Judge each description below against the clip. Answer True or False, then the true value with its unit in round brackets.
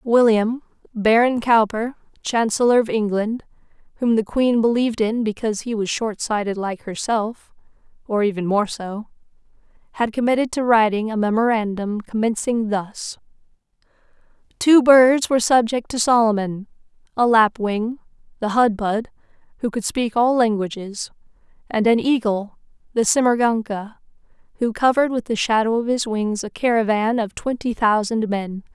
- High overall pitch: True (225 Hz)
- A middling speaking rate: False (130 wpm)